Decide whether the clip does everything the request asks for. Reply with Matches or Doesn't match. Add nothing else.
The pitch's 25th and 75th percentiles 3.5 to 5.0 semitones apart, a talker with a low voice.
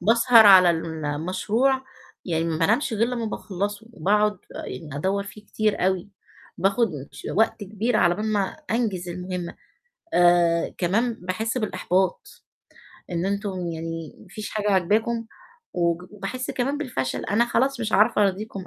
Doesn't match